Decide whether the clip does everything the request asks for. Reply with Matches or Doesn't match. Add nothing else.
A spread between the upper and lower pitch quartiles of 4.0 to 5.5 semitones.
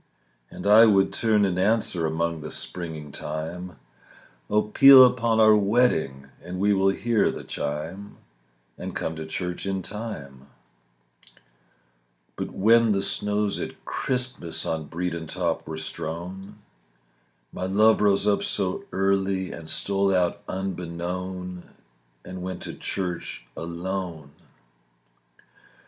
Doesn't match